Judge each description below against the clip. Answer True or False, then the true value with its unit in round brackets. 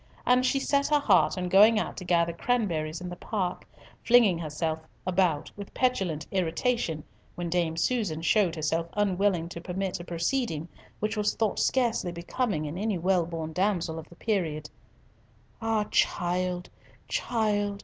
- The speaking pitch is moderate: True (180 Hz)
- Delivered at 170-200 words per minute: False (155 wpm)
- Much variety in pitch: False (4.3 semitones)